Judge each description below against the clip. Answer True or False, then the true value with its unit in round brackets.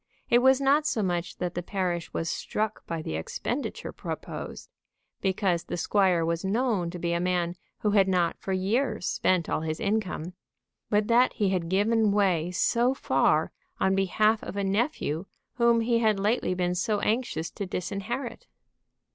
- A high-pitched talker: True (195 Hz)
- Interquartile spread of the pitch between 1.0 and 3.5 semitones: False (4.0 semitones)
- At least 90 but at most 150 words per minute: False (170 wpm)